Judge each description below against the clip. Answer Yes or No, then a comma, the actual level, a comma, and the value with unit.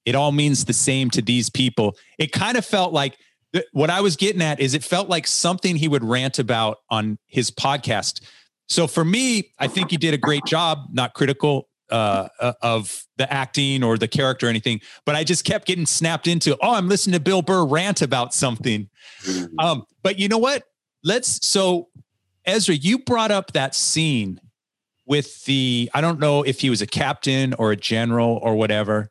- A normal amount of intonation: No, wide, 6.1 semitones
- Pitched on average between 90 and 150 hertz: Yes, medium, 140 Hz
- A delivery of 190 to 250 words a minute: Yes, average, 200 wpm